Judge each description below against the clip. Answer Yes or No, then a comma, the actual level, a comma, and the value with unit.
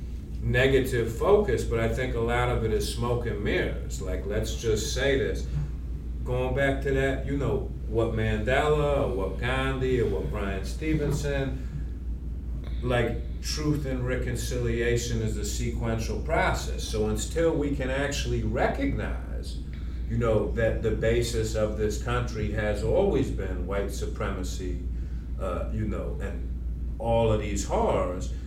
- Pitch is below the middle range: Yes, low, 110 Hz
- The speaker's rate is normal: Yes, average, 145 wpm